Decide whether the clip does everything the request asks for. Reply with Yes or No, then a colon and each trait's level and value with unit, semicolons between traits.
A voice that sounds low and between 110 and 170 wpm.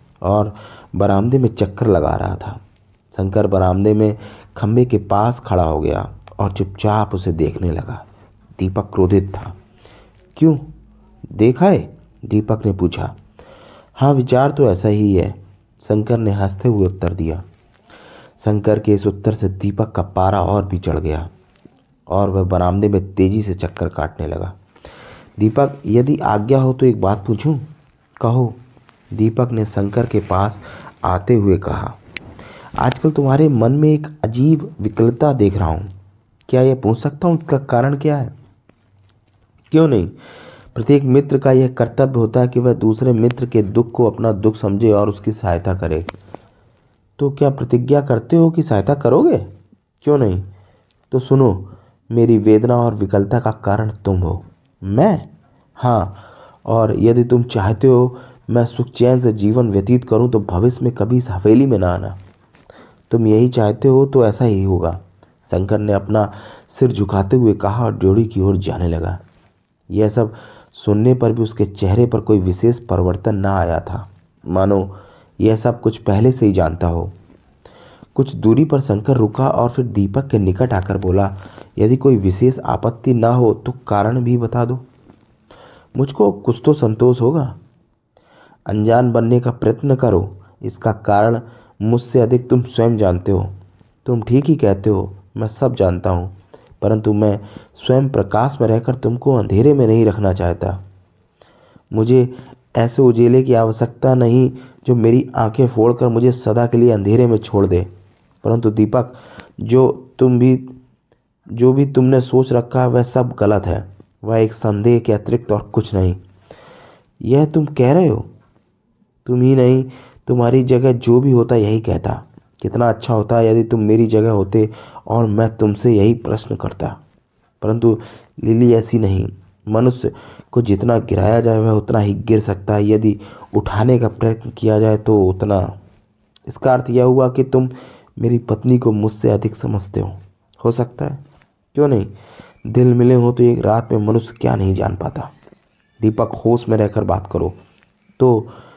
Yes: low, 110 Hz; average, 160 wpm